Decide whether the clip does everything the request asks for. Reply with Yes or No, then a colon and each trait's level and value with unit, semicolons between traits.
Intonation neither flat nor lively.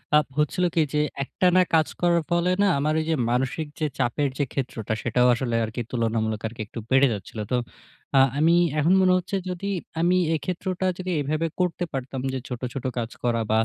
No: wide, 6.1 semitones